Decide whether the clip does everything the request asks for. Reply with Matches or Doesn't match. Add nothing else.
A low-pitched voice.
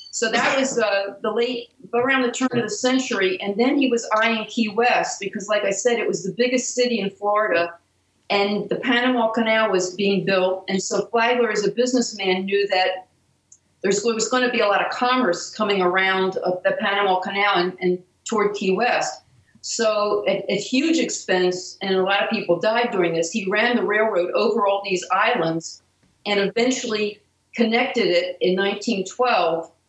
Doesn't match